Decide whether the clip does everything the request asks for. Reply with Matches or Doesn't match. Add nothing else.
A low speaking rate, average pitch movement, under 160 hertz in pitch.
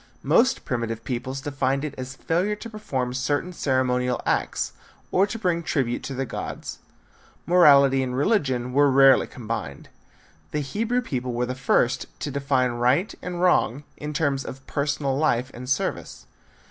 Doesn't match